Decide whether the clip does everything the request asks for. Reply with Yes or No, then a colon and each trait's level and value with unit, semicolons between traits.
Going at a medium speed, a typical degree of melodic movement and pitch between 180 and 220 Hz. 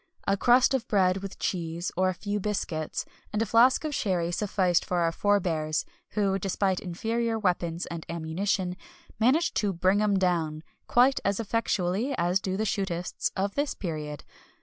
Yes: average, 165 wpm; average, 3.4 semitones; high, 190 Hz